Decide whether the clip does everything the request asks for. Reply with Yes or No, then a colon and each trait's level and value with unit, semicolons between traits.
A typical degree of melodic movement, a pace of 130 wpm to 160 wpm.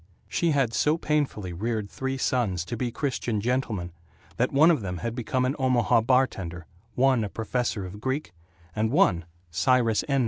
No: average, 4.3 semitones; average, 170 wpm